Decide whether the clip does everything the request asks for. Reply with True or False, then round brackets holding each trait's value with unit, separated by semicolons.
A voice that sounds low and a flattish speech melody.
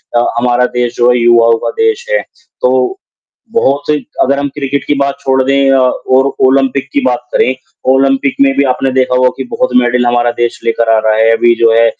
True (130 Hz; 2.3 semitones)